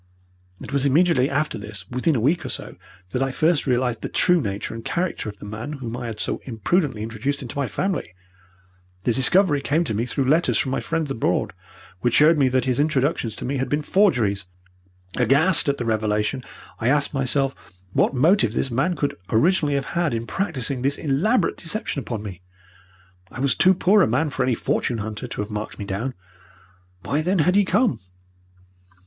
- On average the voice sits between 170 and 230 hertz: No, low, 135 Hz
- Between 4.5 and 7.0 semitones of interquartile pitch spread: Yes, average, 5.2 semitones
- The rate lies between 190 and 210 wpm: Yes, average, 195 wpm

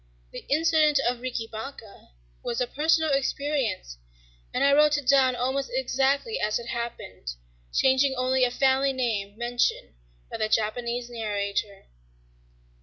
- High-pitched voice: Yes, very high, 255 Hz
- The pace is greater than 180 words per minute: No, slow, 135 wpm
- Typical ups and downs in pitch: Yes, average, 3.7 semitones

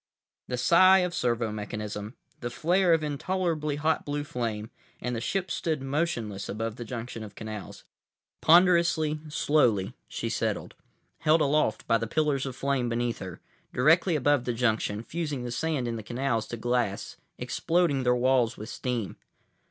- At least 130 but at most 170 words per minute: Yes, average, 160 wpm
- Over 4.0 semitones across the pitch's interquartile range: Yes, average, 5.2 semitones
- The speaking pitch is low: Yes, low, 125 Hz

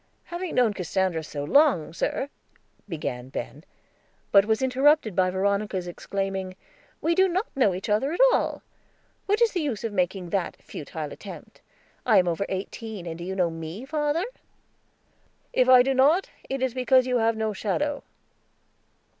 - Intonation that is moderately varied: No, wide, 6.6 semitones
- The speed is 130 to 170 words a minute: Yes, average, 165 wpm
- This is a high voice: Yes, high, 210 Hz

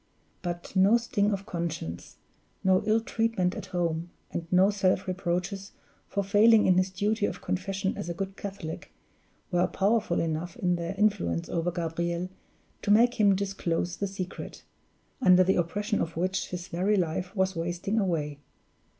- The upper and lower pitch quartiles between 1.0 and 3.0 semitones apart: Yes, average, 2.7 semitones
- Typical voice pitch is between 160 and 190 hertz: Yes, medium, 185 Hz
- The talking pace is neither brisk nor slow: Yes, average, 160 wpm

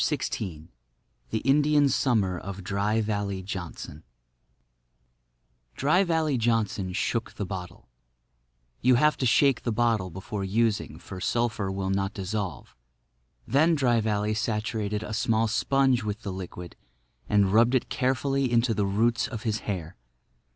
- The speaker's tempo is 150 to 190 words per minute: No, slow, 135 wpm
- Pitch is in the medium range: No, low, 110 Hz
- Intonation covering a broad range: No, average, 3.7 semitones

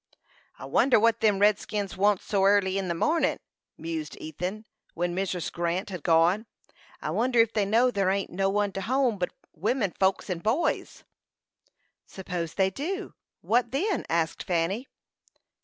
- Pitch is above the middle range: Yes, high, 195 Hz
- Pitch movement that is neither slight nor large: Yes, average, 4.1 semitones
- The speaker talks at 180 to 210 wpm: No, average, 165 wpm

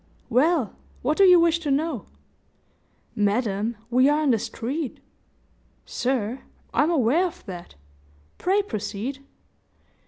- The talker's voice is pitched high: Yes, very high, 265 Hz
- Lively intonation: Yes, wide, 6.1 semitones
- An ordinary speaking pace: No, slow, 120 wpm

